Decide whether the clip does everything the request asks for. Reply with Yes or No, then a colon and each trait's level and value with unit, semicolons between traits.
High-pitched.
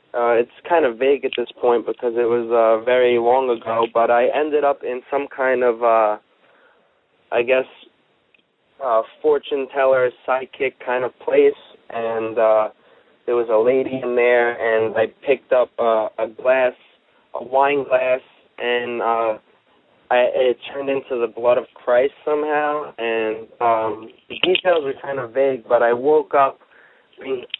No: low, 125 Hz